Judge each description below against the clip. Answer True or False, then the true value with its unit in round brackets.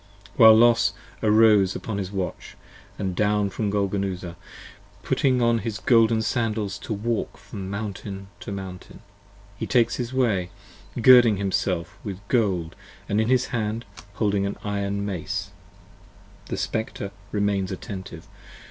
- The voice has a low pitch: True (100 Hz)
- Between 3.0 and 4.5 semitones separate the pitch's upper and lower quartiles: False (2.4 semitones)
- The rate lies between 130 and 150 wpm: True (135 wpm)